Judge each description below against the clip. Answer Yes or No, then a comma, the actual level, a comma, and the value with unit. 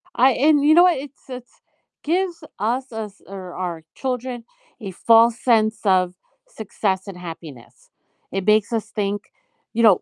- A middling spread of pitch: Yes, average, 5.0 semitones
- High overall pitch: Yes, high, 220 Hz